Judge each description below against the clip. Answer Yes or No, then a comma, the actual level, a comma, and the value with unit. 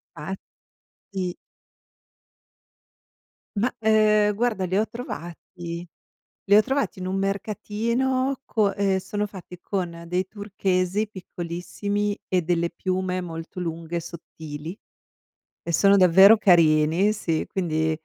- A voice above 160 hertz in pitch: Yes, high, 190 Hz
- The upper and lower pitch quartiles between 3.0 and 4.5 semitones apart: Yes, average, 3.4 semitones